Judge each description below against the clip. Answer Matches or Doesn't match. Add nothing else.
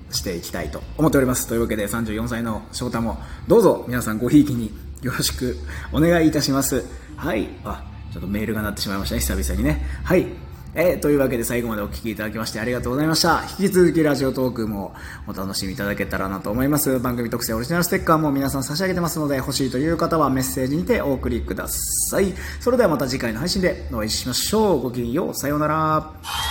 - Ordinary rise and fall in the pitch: Doesn't match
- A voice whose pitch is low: Matches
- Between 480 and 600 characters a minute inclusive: Matches